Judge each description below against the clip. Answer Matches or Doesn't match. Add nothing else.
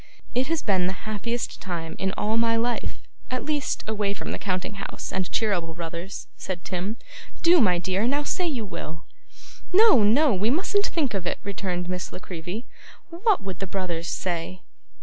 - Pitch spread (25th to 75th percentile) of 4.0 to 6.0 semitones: Matches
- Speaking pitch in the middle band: Doesn't match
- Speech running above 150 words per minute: Matches